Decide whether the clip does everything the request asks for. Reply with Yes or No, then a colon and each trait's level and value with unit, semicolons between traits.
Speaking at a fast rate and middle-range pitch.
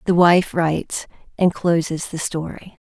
No: average, 145 wpm; medium, 170 Hz